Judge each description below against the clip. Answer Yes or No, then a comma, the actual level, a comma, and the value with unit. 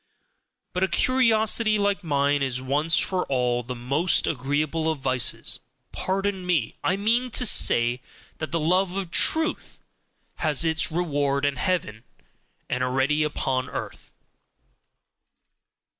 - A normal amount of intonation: No, wide, 5.9 semitones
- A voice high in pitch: No, medium, 155 Hz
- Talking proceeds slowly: Yes, slow, 130 wpm